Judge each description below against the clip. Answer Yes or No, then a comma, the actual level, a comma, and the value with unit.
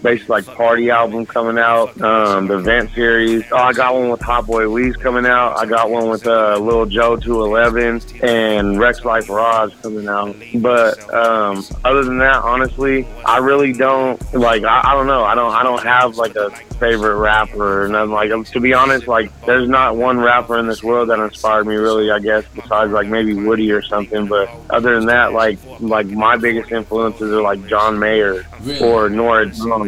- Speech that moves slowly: No, average, 200 wpm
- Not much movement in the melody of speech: Yes, narrow, 2.0 semitones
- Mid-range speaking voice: No, low, 115 Hz